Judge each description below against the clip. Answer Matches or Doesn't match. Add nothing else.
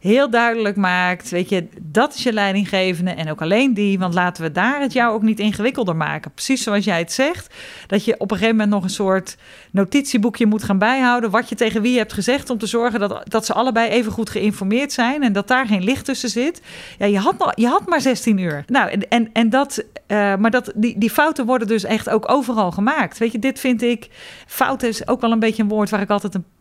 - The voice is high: Matches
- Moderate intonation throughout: Matches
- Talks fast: Matches